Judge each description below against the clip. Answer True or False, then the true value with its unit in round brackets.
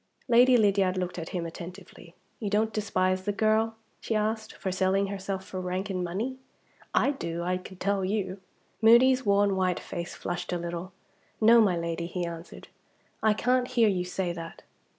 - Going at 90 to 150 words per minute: False (175 wpm)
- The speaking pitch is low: False (190 Hz)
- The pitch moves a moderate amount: True (3.3 semitones)